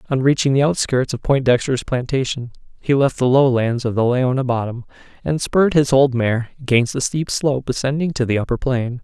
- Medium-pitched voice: No, low, 130 Hz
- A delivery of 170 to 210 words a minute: Yes, average, 200 wpm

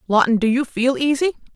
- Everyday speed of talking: Yes, average, 195 wpm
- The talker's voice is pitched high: Yes, very high, 255 Hz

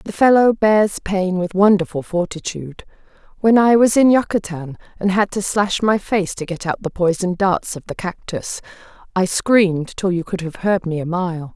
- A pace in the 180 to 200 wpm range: Yes, average, 190 wpm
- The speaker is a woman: Yes, female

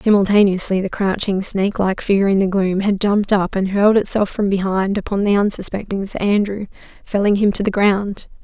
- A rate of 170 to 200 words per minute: Yes, average, 190 wpm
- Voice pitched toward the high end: Yes, high, 200 Hz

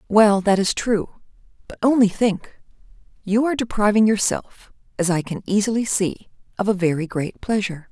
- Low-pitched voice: No, high, 205 Hz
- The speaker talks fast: No, average, 160 wpm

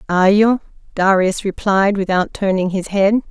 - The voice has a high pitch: Yes, high, 195 Hz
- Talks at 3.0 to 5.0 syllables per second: Yes, 4.9 syllables/s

